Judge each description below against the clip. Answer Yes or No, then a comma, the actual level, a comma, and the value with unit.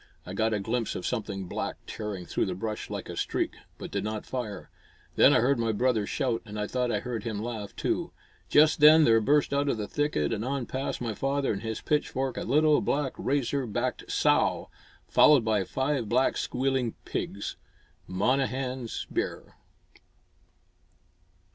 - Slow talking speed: No, average, 175 wpm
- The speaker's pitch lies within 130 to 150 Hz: No, low, 120 Hz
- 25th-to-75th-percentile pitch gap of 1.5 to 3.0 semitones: No, average, 4.1 semitones